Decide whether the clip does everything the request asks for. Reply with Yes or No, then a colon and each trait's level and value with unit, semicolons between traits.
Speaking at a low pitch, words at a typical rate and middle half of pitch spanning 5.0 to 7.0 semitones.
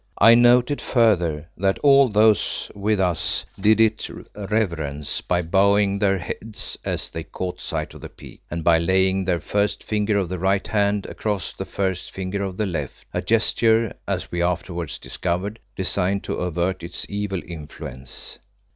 No: very low, 95 Hz; average, 165 wpm; average, 3.1 semitones